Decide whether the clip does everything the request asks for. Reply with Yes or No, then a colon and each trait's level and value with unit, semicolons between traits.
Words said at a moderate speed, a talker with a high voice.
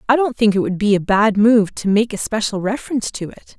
No: fast, 270 wpm; high, 215 Hz